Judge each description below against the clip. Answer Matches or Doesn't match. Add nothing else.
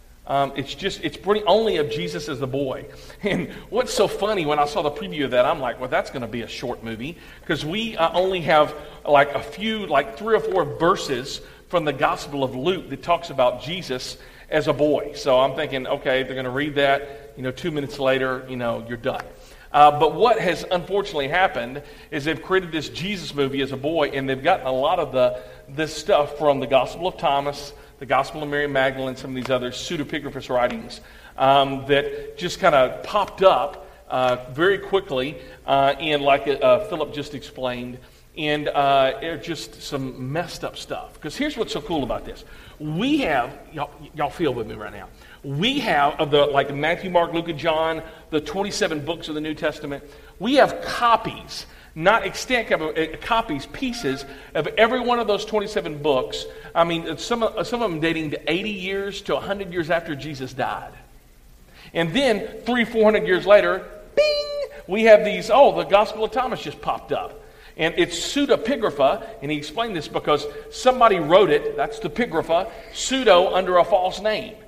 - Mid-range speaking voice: Matches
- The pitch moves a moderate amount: Doesn't match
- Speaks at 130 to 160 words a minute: Doesn't match